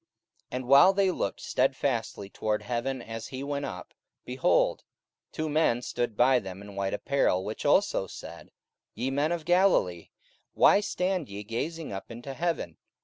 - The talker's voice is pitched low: Yes, low, 130 Hz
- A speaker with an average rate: Yes, average, 165 wpm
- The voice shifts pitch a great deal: Yes, wide, 6.9 semitones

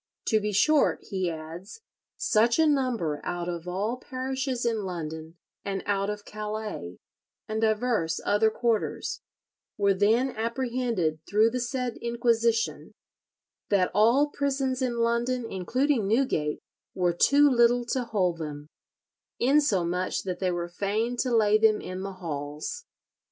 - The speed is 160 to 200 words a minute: No, slow, 135 wpm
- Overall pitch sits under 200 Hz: No, high, 215 Hz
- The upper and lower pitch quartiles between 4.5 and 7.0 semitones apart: Yes, average, 5.1 semitones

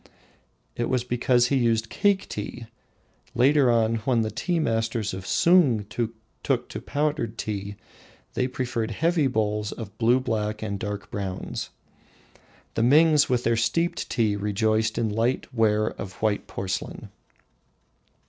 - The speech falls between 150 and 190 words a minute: No, average, 140 wpm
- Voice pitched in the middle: No, low, 115 Hz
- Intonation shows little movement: No, average, 3.0 semitones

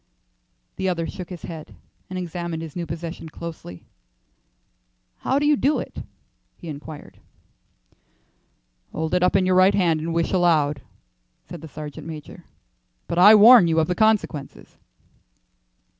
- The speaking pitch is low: No, medium, 170 Hz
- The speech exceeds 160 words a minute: No, average, 145 wpm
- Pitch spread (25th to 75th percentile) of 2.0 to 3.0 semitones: Yes, average, 2.7 semitones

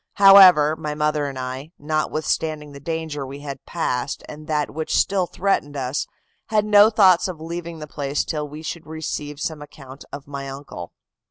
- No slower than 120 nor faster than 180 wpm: Yes, average, 175 wpm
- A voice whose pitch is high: No, medium, 150 Hz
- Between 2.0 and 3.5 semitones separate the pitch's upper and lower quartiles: Yes, narrow, 2.5 semitones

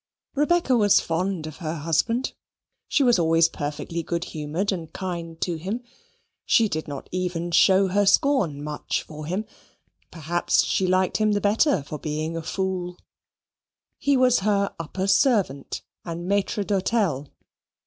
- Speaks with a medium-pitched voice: Yes, medium, 180 Hz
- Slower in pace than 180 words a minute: Yes, average, 150 wpm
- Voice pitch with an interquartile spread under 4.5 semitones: Yes, average, 4.0 semitones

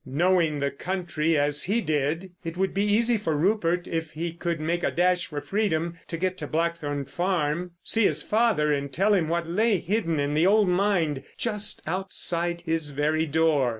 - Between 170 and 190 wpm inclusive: Yes, average, 185 wpm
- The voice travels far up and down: No, average, 3.6 semitones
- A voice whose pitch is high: No, medium, 170 Hz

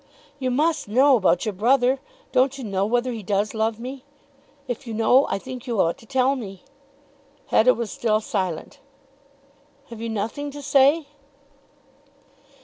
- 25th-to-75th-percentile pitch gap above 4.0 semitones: No, average, 3.6 semitones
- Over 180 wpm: No, average, 155 wpm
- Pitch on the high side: Yes, high, 240 Hz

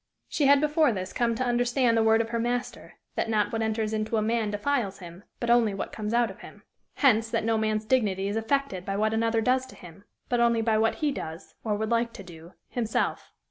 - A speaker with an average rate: No, fast, 235 wpm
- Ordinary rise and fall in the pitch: No, narrow, 2.3 semitones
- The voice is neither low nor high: No, high, 225 Hz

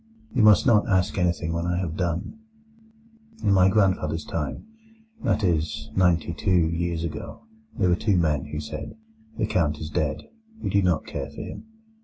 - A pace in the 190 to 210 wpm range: No, average, 165 wpm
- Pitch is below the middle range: Yes, very low, 90 Hz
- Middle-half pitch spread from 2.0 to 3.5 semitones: No, average, 4.2 semitones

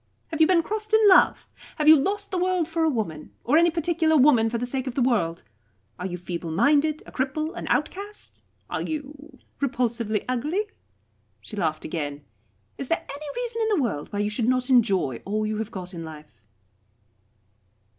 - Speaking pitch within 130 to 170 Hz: No, very high, 260 Hz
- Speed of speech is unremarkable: Yes, average, 185 wpm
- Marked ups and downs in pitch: Yes, wide, 7.6 semitones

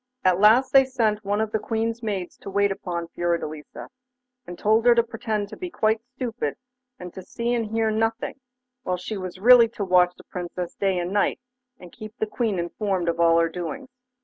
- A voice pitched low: No, high, 210 Hz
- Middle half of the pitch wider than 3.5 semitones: Yes, average, 3.9 semitones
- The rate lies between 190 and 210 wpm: Yes, average, 200 wpm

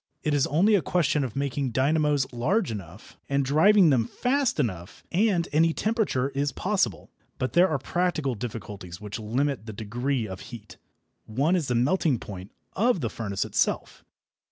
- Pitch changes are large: Yes, wide, 6.8 semitones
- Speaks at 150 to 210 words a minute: Yes, average, 165 wpm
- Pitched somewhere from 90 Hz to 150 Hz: Yes, medium, 140 Hz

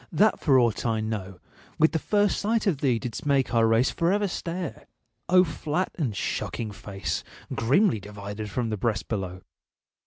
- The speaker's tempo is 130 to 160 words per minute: No, average, 175 wpm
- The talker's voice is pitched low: Yes, low, 125 Hz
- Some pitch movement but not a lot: No, wide, 7.8 semitones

